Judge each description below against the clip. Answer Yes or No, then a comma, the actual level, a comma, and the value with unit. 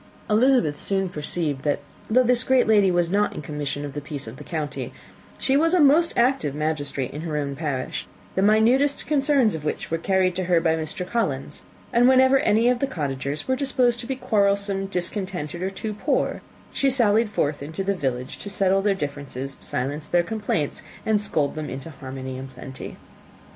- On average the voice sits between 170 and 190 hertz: Yes, medium, 185 Hz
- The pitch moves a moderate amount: No, wide, 7.7 semitones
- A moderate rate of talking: Yes, average, 195 wpm